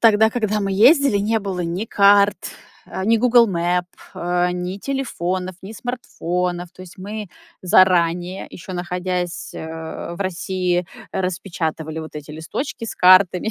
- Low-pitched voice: No, medium, 185 Hz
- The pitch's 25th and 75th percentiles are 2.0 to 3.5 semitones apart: Yes, average, 2.9 semitones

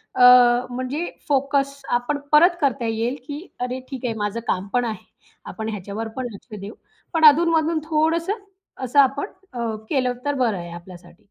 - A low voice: No, very high, 250 Hz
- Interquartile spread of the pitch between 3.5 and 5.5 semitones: Yes, average, 4.4 semitones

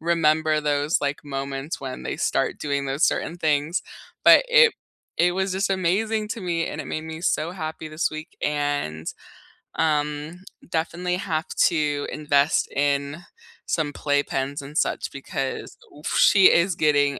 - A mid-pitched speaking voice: Yes, medium, 155 Hz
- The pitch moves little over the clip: No, average, 3.0 semitones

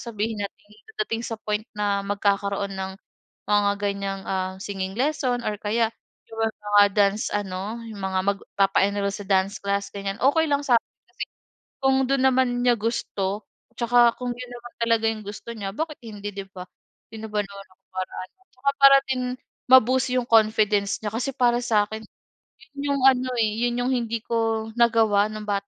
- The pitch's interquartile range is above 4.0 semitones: No, average, 3.2 semitones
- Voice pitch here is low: No, high, 215 Hz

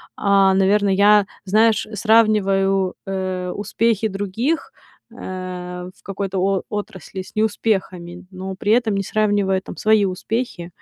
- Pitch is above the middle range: Yes, high, 195 Hz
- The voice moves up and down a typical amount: No, narrow, 2.3 semitones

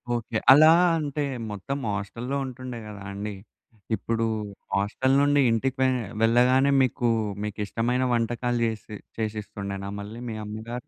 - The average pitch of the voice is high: No, low, 115 Hz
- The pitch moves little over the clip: No, average, 3.5 semitones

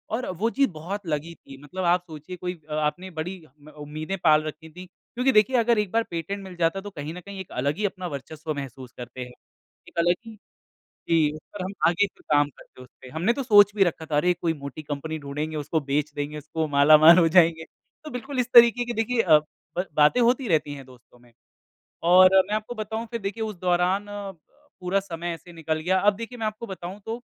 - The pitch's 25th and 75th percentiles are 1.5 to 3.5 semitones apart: No, average, 5.2 semitones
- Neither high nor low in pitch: Yes, medium, 175 Hz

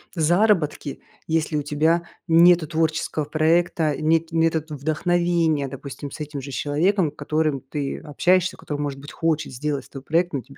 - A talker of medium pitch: Yes, medium, 155 Hz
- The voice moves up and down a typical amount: No, narrow, 2.3 semitones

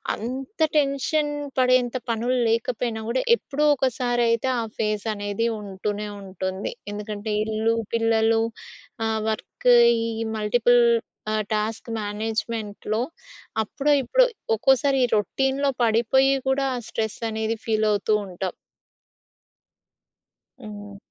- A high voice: Yes, high, 225 Hz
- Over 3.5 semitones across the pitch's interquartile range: No, average, 3.0 semitones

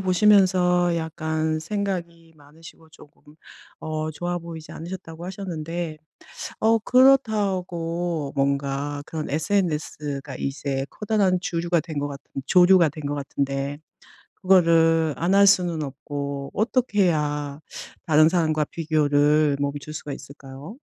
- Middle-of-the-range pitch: Yes, medium, 160 Hz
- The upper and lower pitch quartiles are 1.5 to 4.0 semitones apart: Yes, average, 3.5 semitones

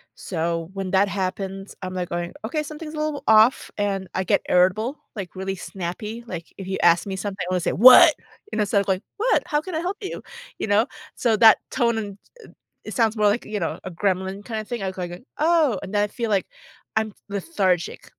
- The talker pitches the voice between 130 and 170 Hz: No, high, 200 Hz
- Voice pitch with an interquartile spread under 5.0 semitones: Yes, average, 3.7 semitones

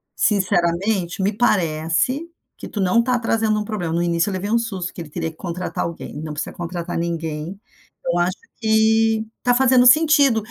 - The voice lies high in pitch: Yes, high, 195 Hz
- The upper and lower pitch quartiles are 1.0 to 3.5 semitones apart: No, average, 4.7 semitones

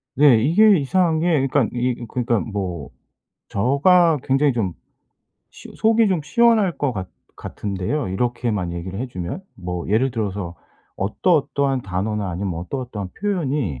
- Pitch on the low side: Yes, low, 120 Hz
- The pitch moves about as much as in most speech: No, wide, 7.5 semitones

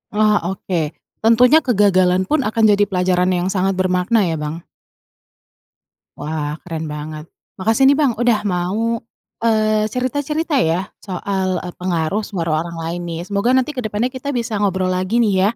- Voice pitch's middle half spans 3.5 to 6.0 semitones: Yes, average, 4.3 semitones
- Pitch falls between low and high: No, high, 195 Hz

